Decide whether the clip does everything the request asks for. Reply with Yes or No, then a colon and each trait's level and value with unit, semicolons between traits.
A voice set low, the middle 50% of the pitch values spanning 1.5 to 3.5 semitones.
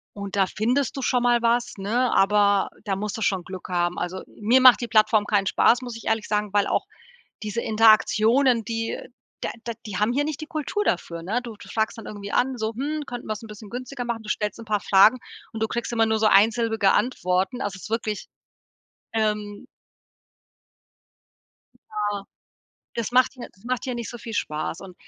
No: high, 220 Hz; average, 2.8 semitones